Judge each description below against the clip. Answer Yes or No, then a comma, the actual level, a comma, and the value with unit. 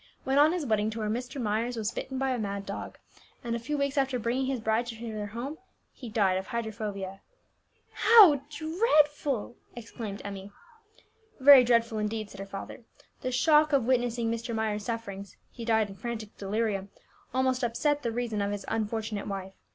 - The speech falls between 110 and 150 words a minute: No, average, 175 wpm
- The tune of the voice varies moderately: Yes, average, 3.7 semitones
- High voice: Yes, high, 230 Hz